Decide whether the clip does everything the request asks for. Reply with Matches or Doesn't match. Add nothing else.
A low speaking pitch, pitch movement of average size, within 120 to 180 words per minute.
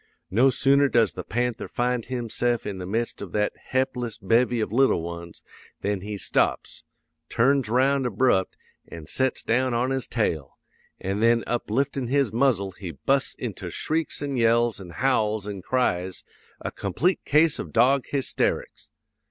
Matches